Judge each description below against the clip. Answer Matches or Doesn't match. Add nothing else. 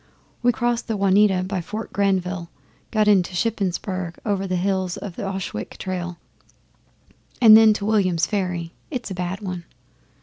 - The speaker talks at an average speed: Matches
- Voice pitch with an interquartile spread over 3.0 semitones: Doesn't match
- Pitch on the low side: Doesn't match